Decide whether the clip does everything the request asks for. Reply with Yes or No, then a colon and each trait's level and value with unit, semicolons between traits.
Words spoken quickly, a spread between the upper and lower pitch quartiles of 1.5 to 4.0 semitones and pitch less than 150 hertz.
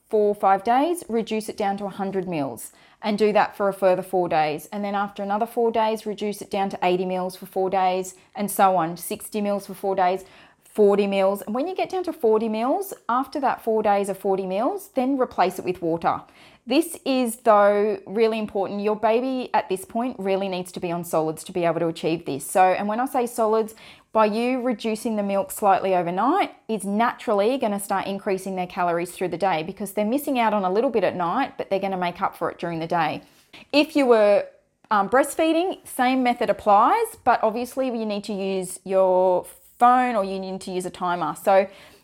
No: fast, 220 wpm; average, 3.6 semitones; high, 205 Hz